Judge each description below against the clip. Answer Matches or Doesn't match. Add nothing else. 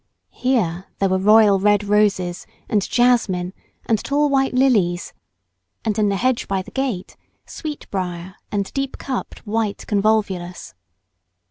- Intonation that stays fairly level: Doesn't match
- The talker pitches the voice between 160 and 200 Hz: Doesn't match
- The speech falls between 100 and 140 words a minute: Matches